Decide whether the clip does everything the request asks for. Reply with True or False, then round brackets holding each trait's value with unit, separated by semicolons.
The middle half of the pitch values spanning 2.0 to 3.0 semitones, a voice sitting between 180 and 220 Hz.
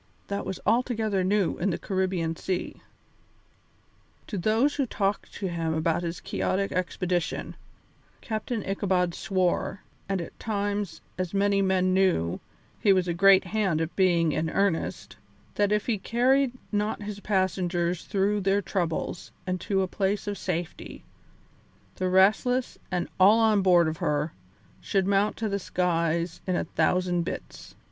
True (2.7 semitones; 190 Hz)